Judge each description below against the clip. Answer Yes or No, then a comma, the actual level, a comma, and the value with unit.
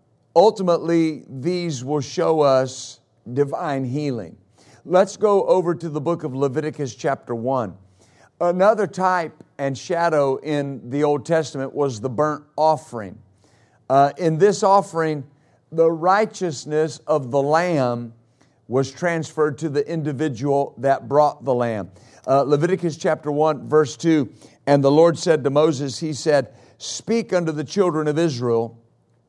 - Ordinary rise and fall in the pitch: Yes, average, 3.8 semitones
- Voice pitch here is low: No, medium, 145 Hz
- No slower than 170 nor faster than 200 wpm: No, slow, 135 wpm